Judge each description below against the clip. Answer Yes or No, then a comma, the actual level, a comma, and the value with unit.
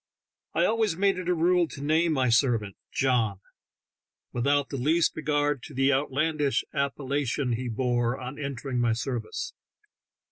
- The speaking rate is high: No, average, 145 wpm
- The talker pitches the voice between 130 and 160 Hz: Yes, medium, 140 Hz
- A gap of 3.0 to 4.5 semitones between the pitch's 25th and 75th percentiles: Yes, average, 3.8 semitones